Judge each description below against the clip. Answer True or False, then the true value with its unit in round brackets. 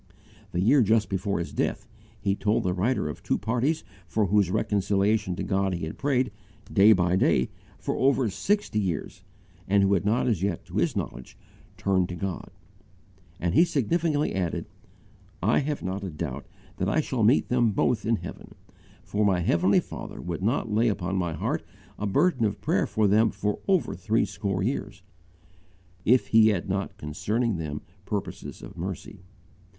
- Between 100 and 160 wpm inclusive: False (175 wpm)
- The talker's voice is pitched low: True (100 Hz)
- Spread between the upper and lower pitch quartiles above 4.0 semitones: False (3.6 semitones)